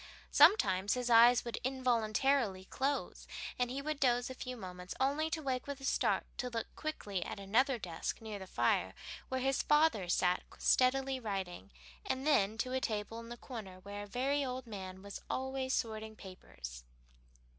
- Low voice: No, high, 240 Hz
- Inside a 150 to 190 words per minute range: Yes, average, 175 wpm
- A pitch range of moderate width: Yes, average, 4.9 semitones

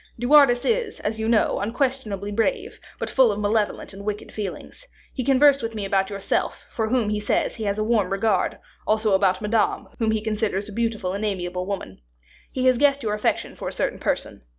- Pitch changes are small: No, average, 3.2 semitones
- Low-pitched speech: No, high, 215 Hz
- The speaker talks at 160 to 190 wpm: No, fast, 205 wpm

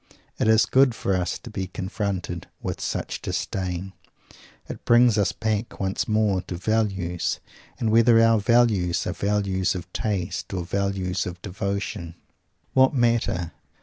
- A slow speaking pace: No, average, 145 wpm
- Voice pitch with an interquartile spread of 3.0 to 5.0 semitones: Yes, average, 3.3 semitones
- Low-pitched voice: Yes, low, 100 Hz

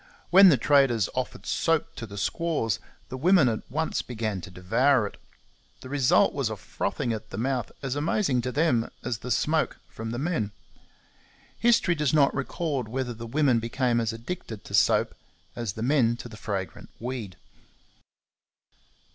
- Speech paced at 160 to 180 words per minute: Yes, average, 165 wpm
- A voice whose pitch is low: Yes, low, 125 Hz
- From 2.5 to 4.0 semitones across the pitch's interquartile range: No, average, 4.4 semitones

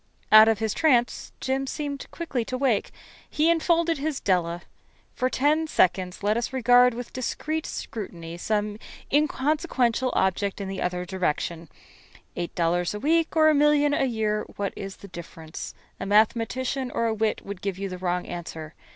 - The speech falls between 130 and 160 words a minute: No, average, 170 wpm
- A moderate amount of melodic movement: No, wide, 6.5 semitones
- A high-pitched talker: Yes, high, 225 Hz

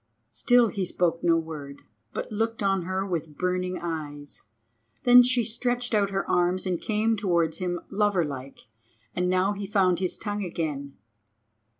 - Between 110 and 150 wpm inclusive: No, average, 160 wpm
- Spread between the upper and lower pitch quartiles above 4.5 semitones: No, average, 3.8 semitones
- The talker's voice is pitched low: No, medium, 185 Hz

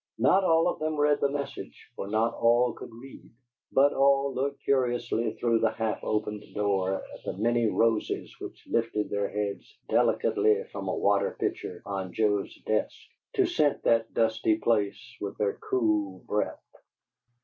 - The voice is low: Yes, low, 115 Hz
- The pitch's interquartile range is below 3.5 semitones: No, average, 4.2 semitones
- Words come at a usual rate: Yes, average, 160 wpm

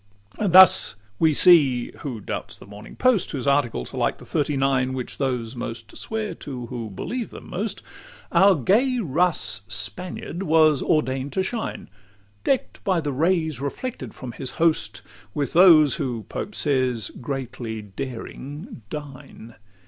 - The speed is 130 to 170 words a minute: Yes, average, 150 wpm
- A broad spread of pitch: Yes, wide, 6.1 semitones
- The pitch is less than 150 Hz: Yes, medium, 140 Hz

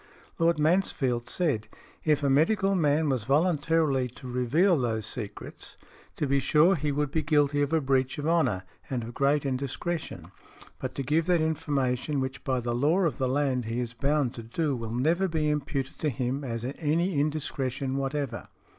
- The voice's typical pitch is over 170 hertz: No, medium, 140 Hz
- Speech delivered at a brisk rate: No, average, 180 wpm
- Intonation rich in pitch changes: No, average, 3.6 semitones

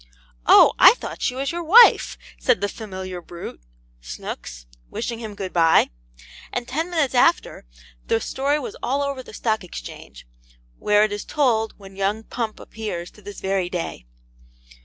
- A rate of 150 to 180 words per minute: Yes, average, 160 wpm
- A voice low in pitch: No, high, 215 Hz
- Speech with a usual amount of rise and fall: No, wide, 5.7 semitones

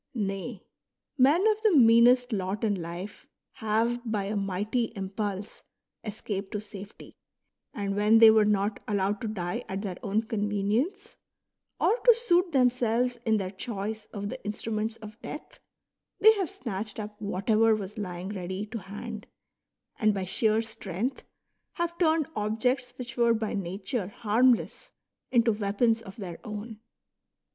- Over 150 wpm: No, average, 145 wpm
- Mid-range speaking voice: No, high, 215 Hz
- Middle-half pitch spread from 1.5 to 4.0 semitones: Yes, average, 3.1 semitones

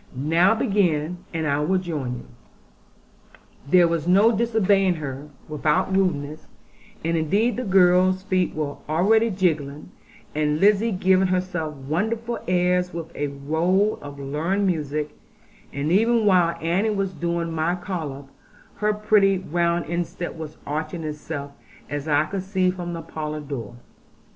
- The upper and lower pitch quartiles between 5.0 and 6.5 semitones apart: No, average, 3.9 semitones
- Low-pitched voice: No, medium, 170 Hz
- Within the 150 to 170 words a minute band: No, average, 140 wpm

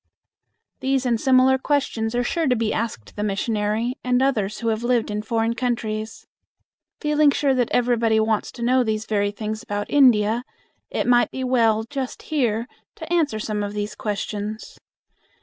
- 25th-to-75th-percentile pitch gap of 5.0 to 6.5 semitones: No, average, 3.1 semitones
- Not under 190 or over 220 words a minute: No, average, 165 wpm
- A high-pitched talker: Yes, high, 230 Hz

